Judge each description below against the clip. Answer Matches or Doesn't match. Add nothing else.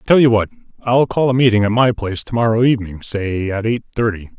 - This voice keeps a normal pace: Doesn't match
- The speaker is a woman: Doesn't match